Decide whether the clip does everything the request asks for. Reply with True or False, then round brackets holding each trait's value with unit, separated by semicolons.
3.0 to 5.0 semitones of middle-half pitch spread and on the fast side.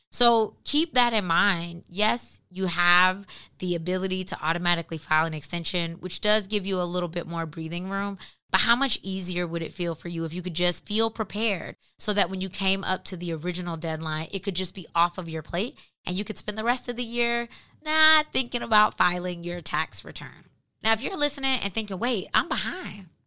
True (3.8 semitones; 215 wpm)